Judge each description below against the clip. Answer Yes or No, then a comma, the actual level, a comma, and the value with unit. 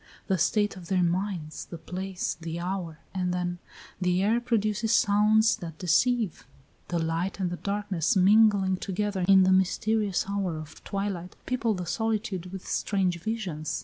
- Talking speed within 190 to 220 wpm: No, average, 155 wpm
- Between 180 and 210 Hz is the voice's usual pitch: Yes, high, 190 Hz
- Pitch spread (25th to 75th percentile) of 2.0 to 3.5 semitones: Yes, average, 2.8 semitones